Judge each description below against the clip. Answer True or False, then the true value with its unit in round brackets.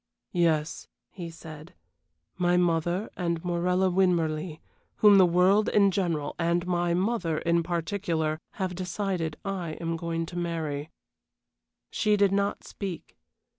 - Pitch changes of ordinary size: False (2.3 semitones)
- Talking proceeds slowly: True (130 wpm)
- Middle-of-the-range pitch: True (175 Hz)